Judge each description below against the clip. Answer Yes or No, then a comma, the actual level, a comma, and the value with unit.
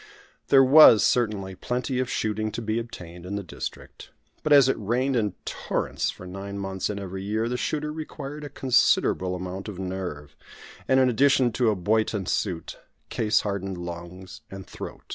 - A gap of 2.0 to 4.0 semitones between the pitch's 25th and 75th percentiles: No, average, 4.8 semitones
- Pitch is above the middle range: No, low, 105 Hz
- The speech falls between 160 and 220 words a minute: Yes, average, 175 wpm